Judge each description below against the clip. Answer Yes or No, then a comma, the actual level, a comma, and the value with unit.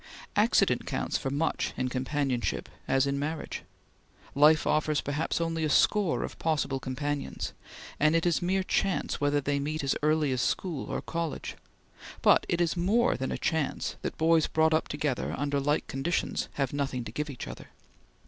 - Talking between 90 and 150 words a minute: No, average, 175 wpm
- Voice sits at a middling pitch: Yes, medium, 150 Hz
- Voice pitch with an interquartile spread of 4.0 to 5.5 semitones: No, average, 2.7 semitones